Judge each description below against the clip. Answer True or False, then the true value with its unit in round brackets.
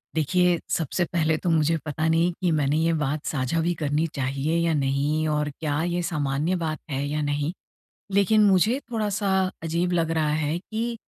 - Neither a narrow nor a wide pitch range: True (3.0 semitones)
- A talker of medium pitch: True (160 Hz)